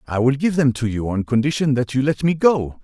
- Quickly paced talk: Yes, fast, 275 wpm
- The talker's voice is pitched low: Yes, low, 130 Hz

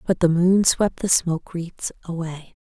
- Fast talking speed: No, average, 185 wpm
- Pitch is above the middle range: No, medium, 175 Hz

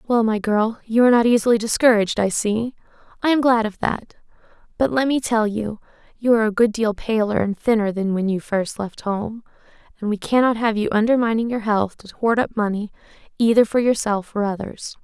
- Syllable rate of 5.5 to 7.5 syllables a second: Yes, 5.6 syllables/s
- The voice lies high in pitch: Yes, high, 220 Hz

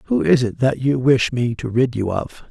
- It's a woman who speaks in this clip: No, male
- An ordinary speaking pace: No, fast, 265 wpm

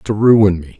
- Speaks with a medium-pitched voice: No, low, 100 Hz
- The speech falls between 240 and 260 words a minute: No, fast, 225 wpm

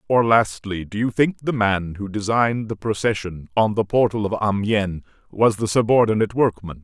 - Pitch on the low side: Yes, low, 105 Hz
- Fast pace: No, average, 175 wpm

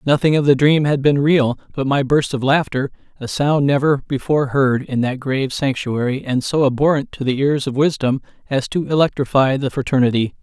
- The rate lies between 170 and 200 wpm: Yes, average, 195 wpm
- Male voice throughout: Yes, male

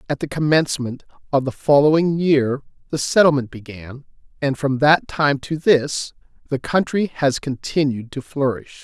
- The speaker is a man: Yes, male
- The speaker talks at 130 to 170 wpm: Yes, average, 150 wpm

